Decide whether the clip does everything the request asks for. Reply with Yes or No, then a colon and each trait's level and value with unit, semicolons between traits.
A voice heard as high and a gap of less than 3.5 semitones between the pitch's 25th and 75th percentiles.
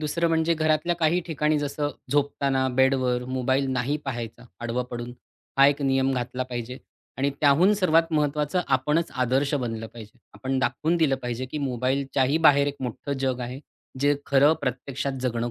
No: low, 135 Hz; average, 2.8 semitones